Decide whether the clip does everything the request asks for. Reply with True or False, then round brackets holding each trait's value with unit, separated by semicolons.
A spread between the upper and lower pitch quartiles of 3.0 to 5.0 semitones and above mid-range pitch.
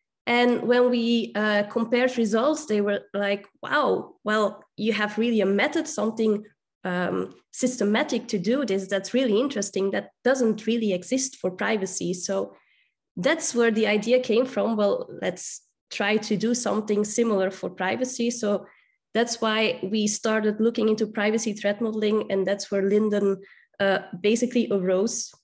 False (2.6 semitones; 215 Hz)